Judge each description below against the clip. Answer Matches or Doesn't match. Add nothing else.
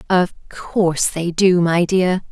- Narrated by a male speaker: Doesn't match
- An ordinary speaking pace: Matches